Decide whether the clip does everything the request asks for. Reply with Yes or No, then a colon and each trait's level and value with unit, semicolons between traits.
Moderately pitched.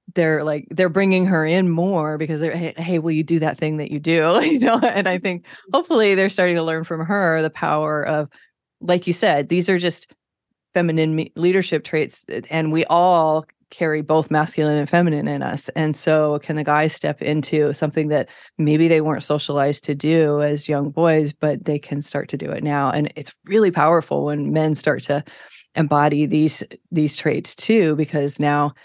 Yes: medium, 155 Hz